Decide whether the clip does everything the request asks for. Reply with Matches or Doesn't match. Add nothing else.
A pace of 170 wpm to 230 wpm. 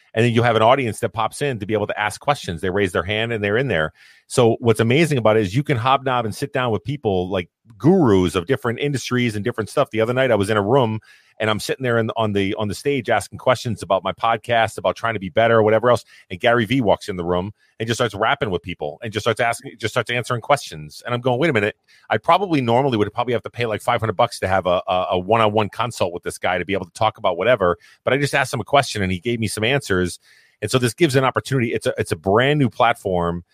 Doesn't match